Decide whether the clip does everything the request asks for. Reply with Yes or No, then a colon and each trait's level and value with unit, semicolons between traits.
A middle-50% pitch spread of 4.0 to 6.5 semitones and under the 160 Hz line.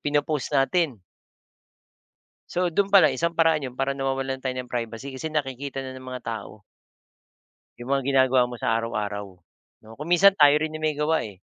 No: average, 3.6 semitones; low, 135 Hz